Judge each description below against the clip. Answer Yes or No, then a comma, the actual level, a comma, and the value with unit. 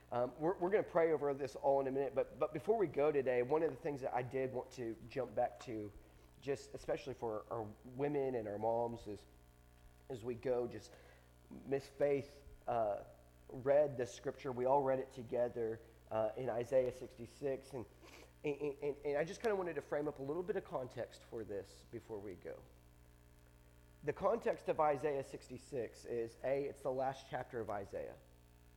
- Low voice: Yes, low, 125 Hz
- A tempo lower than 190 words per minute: No, average, 195 wpm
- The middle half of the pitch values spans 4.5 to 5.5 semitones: Yes, average, 5.0 semitones